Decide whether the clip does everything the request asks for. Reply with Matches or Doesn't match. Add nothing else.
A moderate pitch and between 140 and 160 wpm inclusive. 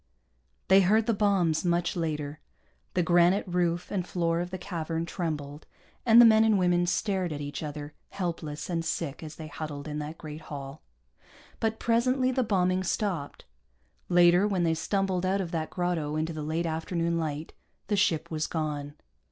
Doesn't match